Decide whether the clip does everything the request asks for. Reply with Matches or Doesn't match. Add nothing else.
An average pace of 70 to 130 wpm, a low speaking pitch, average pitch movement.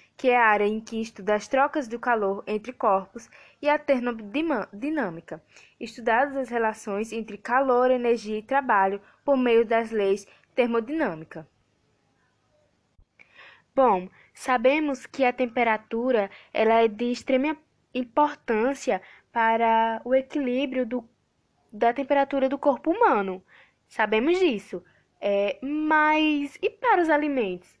Doesn't match